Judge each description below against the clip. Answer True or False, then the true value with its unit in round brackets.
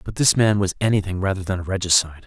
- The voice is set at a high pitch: False (95 Hz)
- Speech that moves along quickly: True (240 wpm)